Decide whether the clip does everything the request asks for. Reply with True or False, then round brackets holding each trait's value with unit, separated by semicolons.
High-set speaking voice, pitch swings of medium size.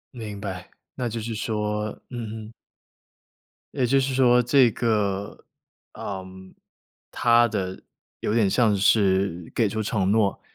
False (105 Hz; 3.1 semitones)